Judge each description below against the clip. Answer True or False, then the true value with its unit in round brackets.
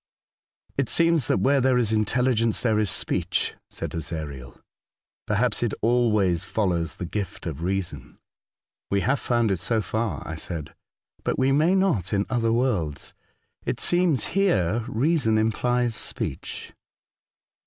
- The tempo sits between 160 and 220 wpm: False (150 wpm)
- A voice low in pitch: True (110 Hz)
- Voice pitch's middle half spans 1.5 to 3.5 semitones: False (5.3 semitones)